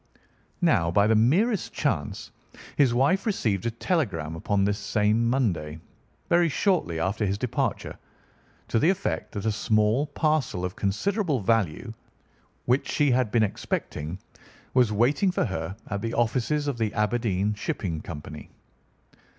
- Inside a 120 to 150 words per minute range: Yes, average, 140 wpm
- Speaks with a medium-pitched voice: No, low, 110 Hz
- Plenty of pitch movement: Yes, wide, 5.9 semitones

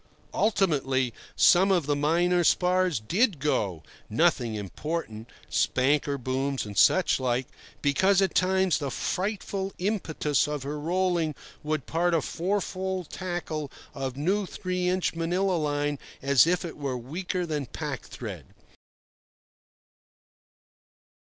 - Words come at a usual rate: No, slow, 115 wpm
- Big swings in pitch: No, average, 4.9 semitones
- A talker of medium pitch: Yes, medium, 160 Hz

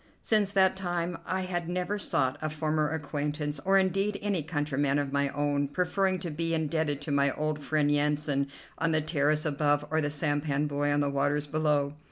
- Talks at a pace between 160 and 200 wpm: Yes, average, 190 wpm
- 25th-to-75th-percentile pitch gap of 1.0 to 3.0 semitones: Yes, narrow, 2.5 semitones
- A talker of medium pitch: Yes, medium, 150 Hz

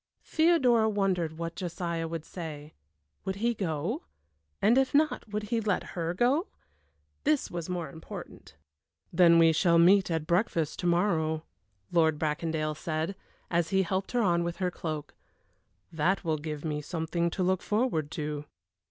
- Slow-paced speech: No, average, 155 wpm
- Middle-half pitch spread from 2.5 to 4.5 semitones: Yes, average, 3.7 semitones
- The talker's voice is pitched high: No, medium, 170 Hz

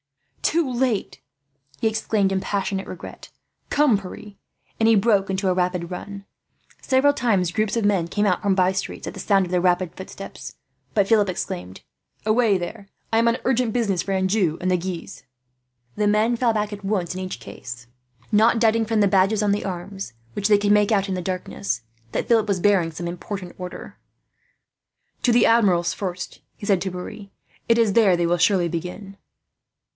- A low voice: No, high, 195 Hz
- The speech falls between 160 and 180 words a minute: No, average, 190 wpm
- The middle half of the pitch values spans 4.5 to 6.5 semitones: No, average, 3.2 semitones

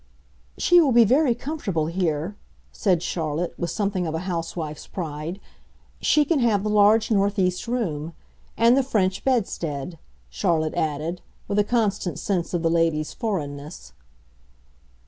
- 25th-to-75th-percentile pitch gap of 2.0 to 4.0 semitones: No, average, 5.1 semitones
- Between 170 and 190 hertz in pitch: Yes, medium, 185 Hz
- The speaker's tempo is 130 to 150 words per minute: Yes, average, 140 wpm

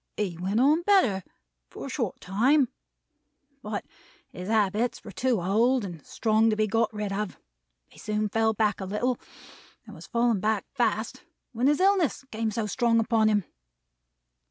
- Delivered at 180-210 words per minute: No, average, 165 wpm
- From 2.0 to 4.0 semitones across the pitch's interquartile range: Yes, average, 2.7 semitones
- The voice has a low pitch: No, high, 220 Hz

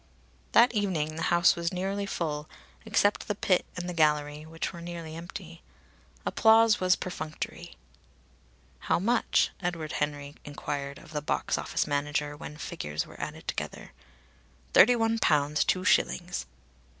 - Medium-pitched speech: Yes, medium, 165 Hz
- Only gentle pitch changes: No, average, 3.9 semitones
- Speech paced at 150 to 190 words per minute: No, average, 140 wpm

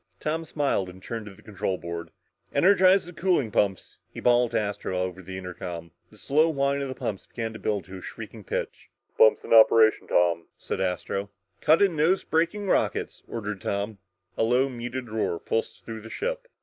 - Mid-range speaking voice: No, low, 110 Hz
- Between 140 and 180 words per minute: No, average, 190 wpm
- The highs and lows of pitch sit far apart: Yes, wide, 7.5 semitones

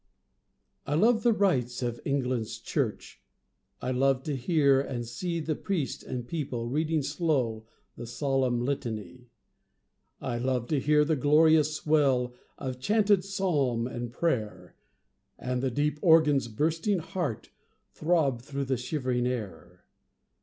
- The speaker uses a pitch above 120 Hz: Yes, low, 135 Hz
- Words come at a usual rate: No, slow, 130 wpm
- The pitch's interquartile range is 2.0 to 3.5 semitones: No, average, 4.3 semitones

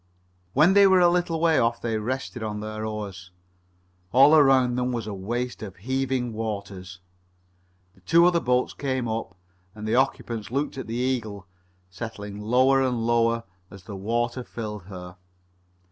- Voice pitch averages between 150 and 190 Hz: No, low, 115 Hz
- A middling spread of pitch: Yes, average, 3.7 semitones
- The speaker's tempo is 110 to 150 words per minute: No, average, 160 wpm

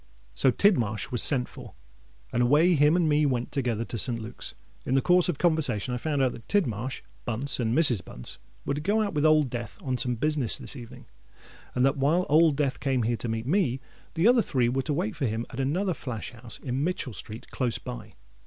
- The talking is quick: Yes, fast, 220 wpm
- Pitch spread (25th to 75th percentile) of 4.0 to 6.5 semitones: Yes, average, 4.4 semitones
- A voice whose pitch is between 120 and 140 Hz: Yes, low, 135 Hz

